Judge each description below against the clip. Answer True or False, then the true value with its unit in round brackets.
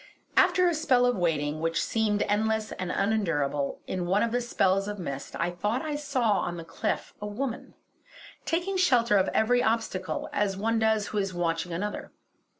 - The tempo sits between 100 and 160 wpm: False (180 wpm)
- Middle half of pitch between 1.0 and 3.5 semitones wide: False (5.1 semitones)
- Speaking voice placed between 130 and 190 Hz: False (210 Hz)